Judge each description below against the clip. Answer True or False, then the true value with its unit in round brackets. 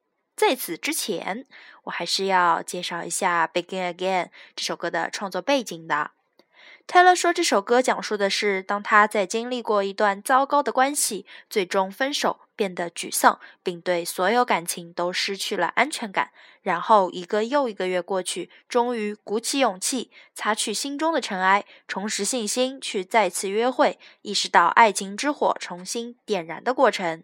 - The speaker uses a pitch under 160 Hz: False (210 Hz)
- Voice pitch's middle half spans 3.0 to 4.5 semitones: False (5.1 semitones)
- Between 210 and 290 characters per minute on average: True (265 characters per minute)